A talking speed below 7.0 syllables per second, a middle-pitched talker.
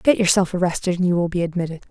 No: 7.1 syllables/s; medium, 180 Hz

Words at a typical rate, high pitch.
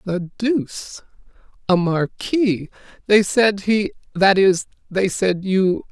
No: slow, 110 wpm; high, 195 Hz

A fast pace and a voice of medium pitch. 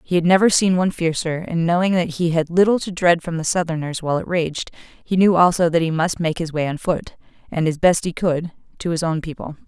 Yes: fast, 250 wpm; medium, 170 Hz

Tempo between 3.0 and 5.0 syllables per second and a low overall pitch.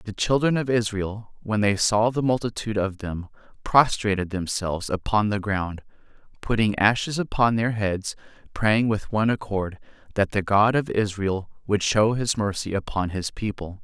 Yes: 4.8 syllables/s; low, 105 Hz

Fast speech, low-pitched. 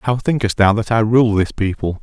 Yes: fast, 240 wpm; low, 110 Hz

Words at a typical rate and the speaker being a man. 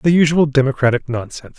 Yes: average, 150 wpm; male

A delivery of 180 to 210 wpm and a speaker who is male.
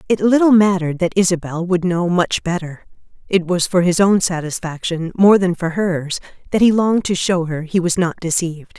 No: average, 200 wpm; female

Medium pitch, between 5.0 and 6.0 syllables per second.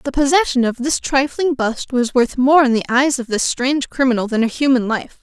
No: very high, 260 Hz; 5.4 syllables/s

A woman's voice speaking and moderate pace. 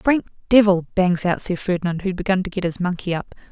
No: female; fast, 220 wpm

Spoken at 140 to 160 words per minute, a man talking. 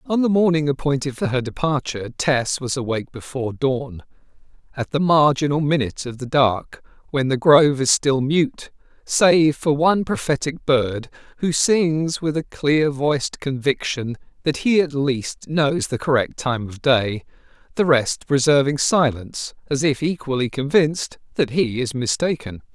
Yes: average, 155 wpm; male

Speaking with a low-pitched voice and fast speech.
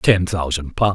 No: very low, 90 Hz; average, 190 wpm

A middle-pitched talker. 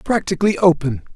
Yes: medium, 170 Hz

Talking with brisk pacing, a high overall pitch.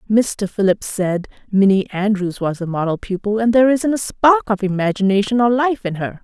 No: average, 195 wpm; high, 210 Hz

